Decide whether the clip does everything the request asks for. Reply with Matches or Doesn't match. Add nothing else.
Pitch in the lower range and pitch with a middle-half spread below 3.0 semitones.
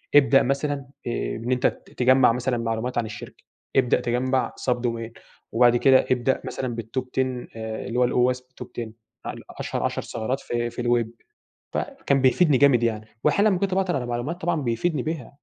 Matches